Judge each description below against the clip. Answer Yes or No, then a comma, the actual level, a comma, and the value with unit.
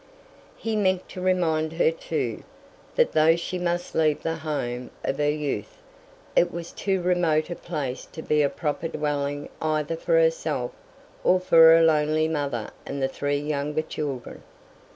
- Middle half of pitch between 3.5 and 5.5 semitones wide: No, average, 3.1 semitones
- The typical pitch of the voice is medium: Yes, medium, 155 Hz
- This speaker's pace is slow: No, average, 160 wpm